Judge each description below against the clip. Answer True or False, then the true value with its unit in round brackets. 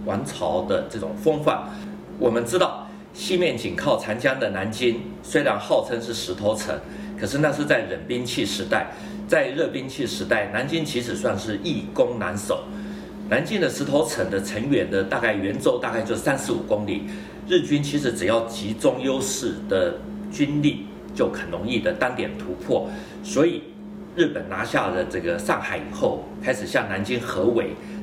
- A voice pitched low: True (120 Hz)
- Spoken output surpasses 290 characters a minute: False (255 characters per minute)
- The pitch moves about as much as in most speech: False (7.0 semitones)